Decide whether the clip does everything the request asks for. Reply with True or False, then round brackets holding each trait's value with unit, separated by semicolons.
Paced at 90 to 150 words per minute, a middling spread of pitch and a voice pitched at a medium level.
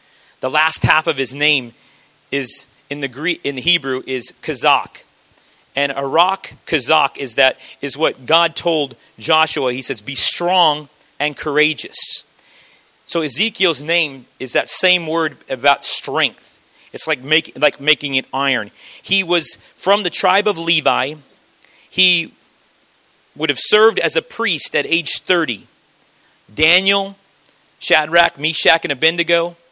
True (140 wpm; 3.5 semitones; 155 Hz)